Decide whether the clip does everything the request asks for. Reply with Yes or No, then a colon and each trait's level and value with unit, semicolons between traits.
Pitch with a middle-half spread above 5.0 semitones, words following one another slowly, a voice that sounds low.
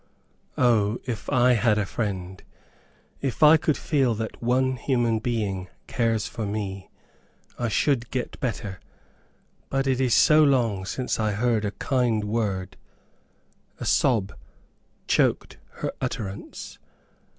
No: average, 3.5 semitones; slow, 130 wpm; low, 115 Hz